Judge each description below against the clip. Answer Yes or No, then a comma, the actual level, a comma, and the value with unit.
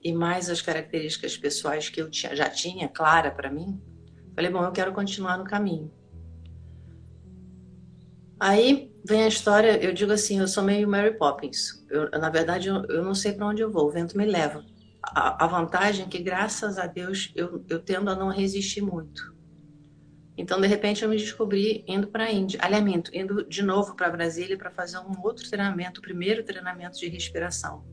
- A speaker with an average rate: No, fast, 190 wpm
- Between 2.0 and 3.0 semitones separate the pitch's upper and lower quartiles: No, average, 4.5 semitones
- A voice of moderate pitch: Yes, medium, 180 Hz